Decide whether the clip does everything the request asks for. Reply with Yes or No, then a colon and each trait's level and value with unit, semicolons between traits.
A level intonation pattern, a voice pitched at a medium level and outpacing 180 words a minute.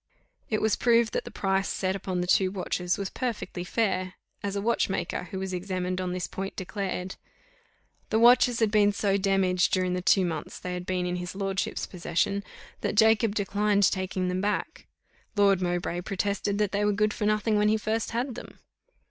No: narrow, 2.3 semitones; high, 195 Hz; average, 190 wpm